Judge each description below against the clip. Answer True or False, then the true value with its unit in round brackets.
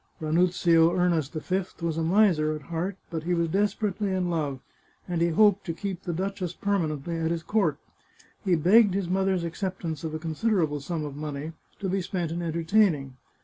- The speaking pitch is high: False (170 Hz)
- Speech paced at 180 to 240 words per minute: True (190 wpm)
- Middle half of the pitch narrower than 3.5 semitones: True (3.1 semitones)